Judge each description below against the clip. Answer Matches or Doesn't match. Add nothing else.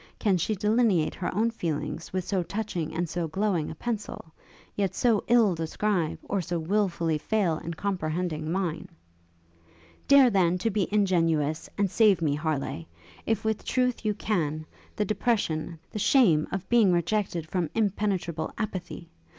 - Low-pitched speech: Doesn't match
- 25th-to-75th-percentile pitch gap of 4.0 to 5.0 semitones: Matches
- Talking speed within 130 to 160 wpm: Matches